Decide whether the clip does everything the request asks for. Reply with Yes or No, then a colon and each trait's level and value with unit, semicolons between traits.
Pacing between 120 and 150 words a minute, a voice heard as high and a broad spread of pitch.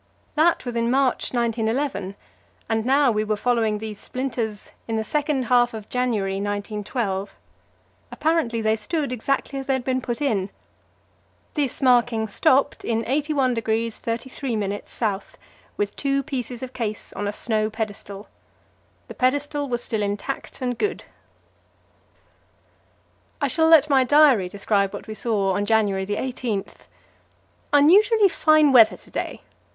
No: average, 140 wpm; high, 235 Hz; average, 4.2 semitones